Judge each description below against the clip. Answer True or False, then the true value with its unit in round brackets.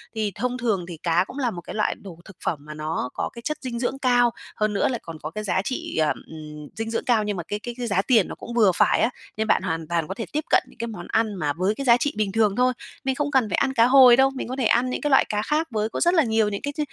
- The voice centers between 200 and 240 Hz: True (220 Hz)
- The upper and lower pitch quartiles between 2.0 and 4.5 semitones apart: False (4.9 semitones)